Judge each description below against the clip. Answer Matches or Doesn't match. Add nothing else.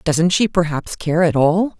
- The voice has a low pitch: Doesn't match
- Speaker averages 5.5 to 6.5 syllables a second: Doesn't match